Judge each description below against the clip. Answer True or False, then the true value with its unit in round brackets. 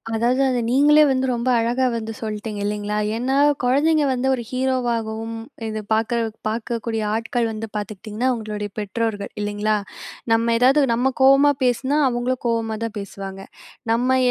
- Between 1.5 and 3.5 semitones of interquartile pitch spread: True (2.9 semitones)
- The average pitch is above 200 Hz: True (230 Hz)